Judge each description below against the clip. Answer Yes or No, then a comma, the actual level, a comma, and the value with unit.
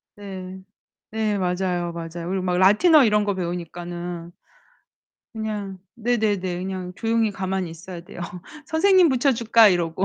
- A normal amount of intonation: Yes, average, 3.6 semitones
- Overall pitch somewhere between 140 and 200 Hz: Yes, high, 190 Hz